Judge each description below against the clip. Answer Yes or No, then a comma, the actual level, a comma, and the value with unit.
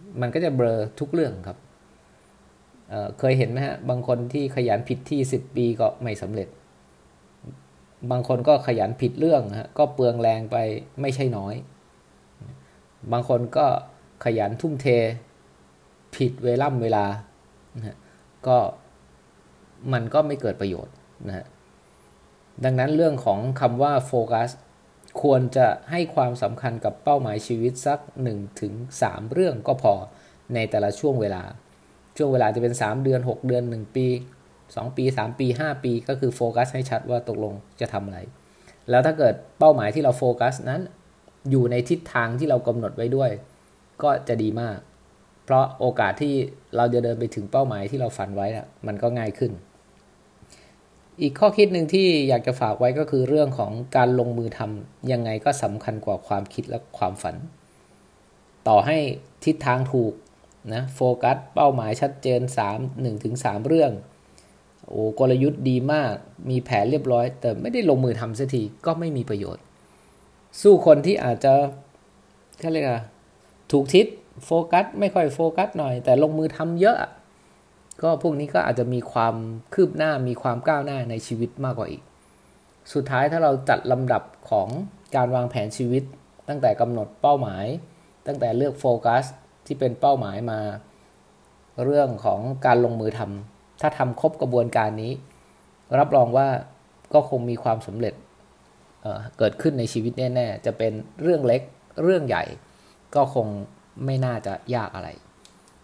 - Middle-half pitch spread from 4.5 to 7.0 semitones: No, average, 4.1 semitones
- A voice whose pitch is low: Yes, low, 120 Hz